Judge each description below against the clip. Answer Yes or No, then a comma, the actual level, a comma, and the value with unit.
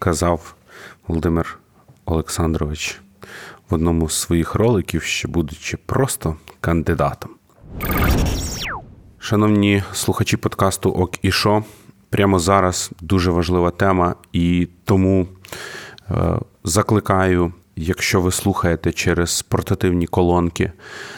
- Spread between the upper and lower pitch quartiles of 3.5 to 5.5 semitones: No, average, 2.7 semitones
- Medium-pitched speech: No, very low, 90 Hz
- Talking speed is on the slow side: Yes, slow, 90 wpm